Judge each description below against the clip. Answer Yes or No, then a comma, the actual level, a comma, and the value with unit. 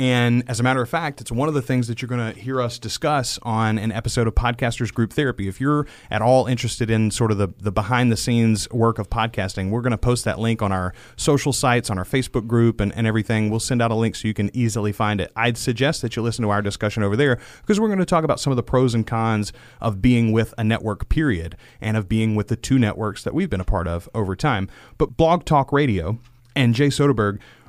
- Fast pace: Yes, fast, 260 wpm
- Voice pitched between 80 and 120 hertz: Yes, low, 115 Hz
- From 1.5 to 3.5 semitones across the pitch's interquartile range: Yes, average, 2.9 semitones